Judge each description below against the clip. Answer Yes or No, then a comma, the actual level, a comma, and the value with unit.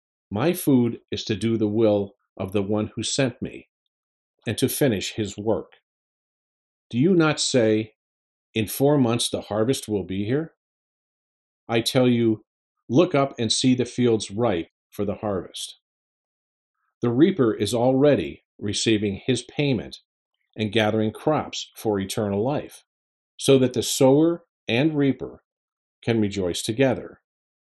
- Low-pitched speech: Yes, low, 110 Hz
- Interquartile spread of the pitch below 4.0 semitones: No, average, 4.4 semitones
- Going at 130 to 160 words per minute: Yes, average, 140 wpm